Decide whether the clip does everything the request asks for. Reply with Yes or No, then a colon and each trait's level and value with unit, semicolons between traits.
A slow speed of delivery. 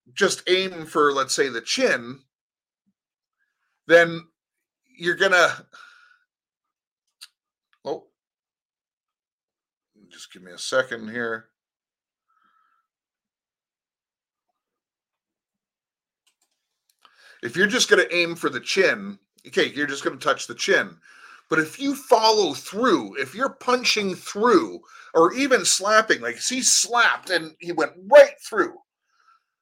Yes: slow, 105 wpm